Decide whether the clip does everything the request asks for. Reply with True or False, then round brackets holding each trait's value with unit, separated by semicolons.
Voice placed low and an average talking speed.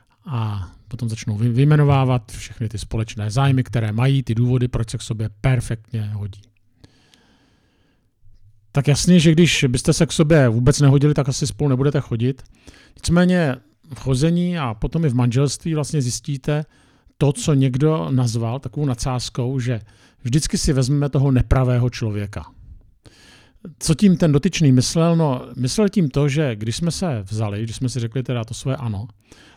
True (130 Hz; 160 wpm)